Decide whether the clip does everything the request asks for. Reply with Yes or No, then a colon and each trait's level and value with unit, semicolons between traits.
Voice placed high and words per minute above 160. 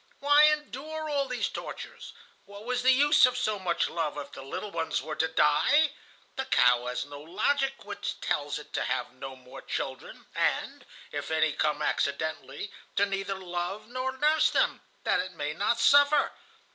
Yes: high, 200 Hz; average, 175 wpm